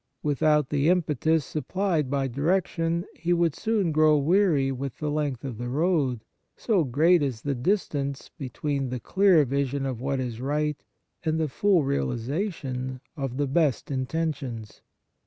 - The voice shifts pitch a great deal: No, average, 3.7 semitones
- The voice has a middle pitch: Yes, medium, 145 Hz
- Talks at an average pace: Yes, average, 145 wpm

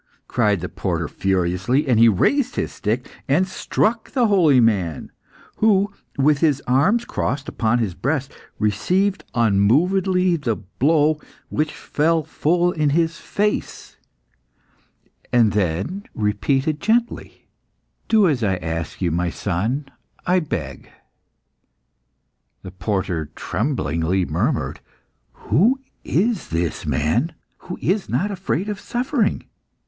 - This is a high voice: No, medium, 140 Hz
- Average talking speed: No, slow, 120 wpm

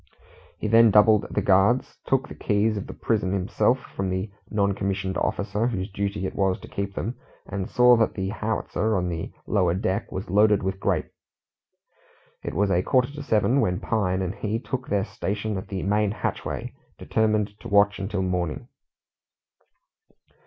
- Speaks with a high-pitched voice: No, low, 100 Hz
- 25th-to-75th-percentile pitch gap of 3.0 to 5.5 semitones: No, narrow, 2.4 semitones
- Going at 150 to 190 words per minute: Yes, average, 175 wpm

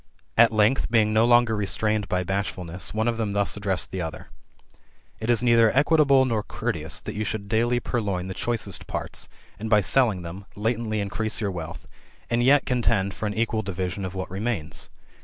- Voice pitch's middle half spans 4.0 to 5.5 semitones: No, average, 3.4 semitones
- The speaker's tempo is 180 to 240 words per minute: Yes, average, 190 wpm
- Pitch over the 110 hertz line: No, low, 105 Hz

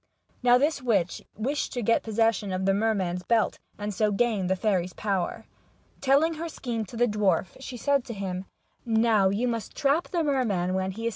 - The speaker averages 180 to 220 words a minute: Yes, average, 200 wpm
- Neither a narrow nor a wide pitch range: Yes, average, 4.2 semitones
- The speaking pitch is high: Yes, high, 220 Hz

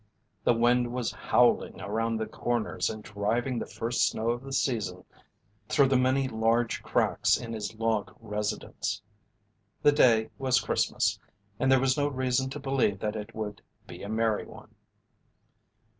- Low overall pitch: Yes, low, 115 Hz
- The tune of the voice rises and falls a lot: No, average, 2.9 semitones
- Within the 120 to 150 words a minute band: No, average, 160 wpm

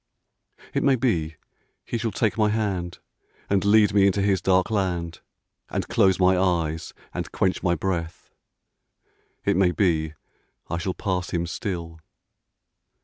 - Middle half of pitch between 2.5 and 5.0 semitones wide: Yes, average, 2.9 semitones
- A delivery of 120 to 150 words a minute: Yes, average, 145 wpm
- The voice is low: Yes, very low, 95 Hz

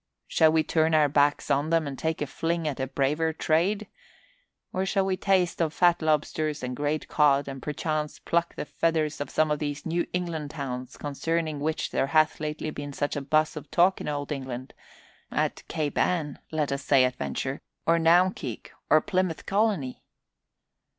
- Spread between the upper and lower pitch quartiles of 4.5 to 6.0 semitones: No, narrow, 2.5 semitones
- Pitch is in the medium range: Yes, medium, 155 Hz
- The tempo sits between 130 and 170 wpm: No, average, 185 wpm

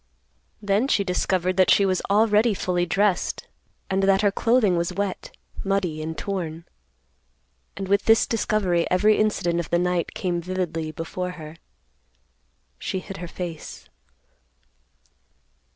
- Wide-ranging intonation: No, narrow, 2.6 semitones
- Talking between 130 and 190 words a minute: Yes, slow, 135 wpm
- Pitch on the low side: No, medium, 185 Hz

